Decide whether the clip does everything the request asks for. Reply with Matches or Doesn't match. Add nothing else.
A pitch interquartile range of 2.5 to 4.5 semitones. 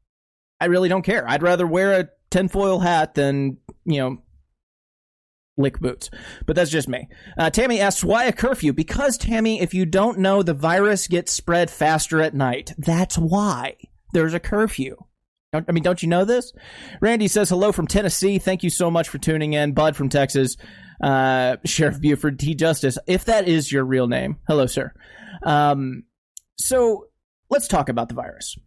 Doesn't match